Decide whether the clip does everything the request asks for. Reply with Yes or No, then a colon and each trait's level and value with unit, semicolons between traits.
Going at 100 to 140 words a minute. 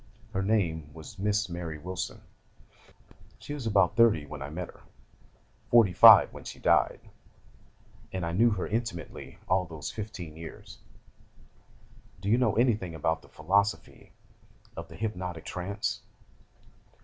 Yes: slow, 135 wpm